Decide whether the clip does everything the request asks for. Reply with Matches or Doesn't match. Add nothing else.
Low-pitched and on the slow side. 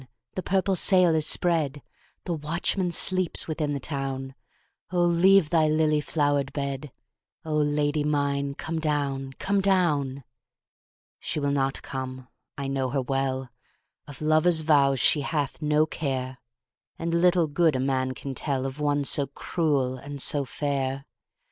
Doesn't match